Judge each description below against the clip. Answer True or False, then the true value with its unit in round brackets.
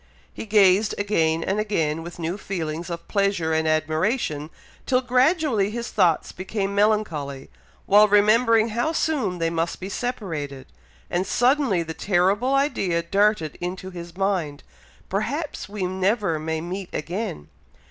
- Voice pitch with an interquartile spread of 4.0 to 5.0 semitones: True (4.5 semitones)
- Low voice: False (190 Hz)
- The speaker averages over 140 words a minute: False (135 wpm)